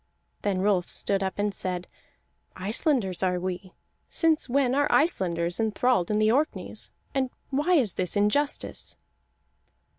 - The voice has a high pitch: Yes, high, 210 Hz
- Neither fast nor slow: No, slow, 130 wpm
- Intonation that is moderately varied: No, wide, 6.5 semitones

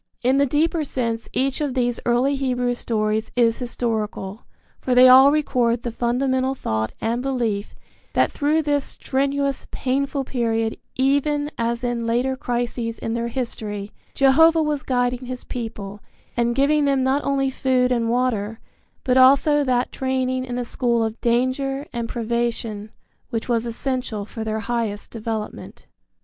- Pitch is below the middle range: No, high, 245 Hz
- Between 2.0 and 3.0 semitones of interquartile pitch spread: Yes, average, 2.7 semitones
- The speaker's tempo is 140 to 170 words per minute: Yes, average, 150 wpm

